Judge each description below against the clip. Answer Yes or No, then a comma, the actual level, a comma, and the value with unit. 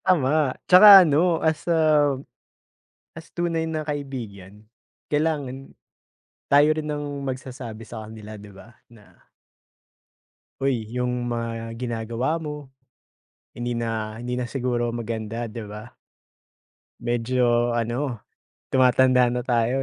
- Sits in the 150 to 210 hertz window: No, low, 125 Hz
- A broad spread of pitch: No, average, 4.2 semitones